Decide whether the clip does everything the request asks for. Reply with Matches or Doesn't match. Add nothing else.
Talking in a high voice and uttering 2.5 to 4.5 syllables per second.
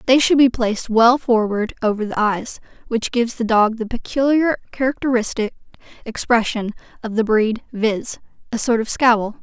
Doesn't match